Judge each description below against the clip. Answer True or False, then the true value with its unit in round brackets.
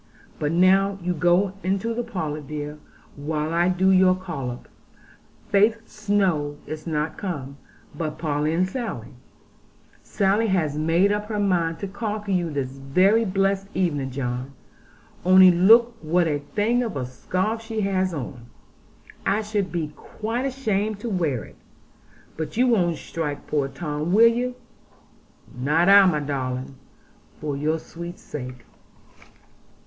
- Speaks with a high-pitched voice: False (175 Hz)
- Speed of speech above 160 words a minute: False (145 wpm)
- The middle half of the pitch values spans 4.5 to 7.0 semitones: True (5.3 semitones)